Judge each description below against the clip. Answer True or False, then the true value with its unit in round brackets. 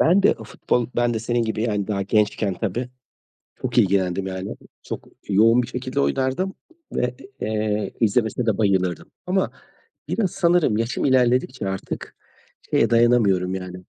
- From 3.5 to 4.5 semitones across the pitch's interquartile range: True (4.2 semitones)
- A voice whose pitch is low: True (115 Hz)